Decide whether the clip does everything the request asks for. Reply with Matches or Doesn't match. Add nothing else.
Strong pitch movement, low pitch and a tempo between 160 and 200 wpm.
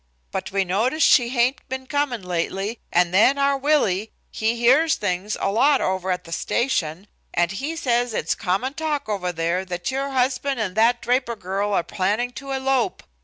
Doesn't match